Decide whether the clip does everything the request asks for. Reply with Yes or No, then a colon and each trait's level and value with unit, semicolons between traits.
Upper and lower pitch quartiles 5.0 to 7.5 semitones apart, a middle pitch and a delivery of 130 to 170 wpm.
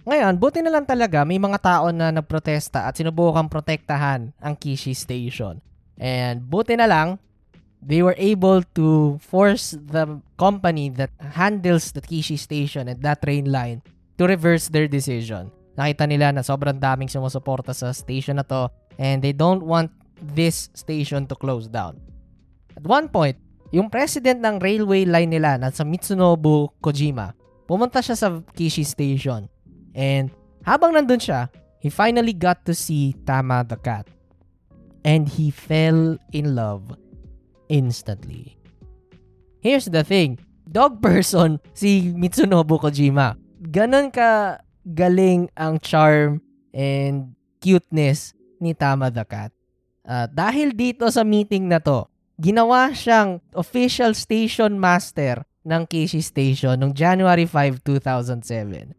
Yes: wide, 5.4 semitones; medium, 155 Hz; average, 135 wpm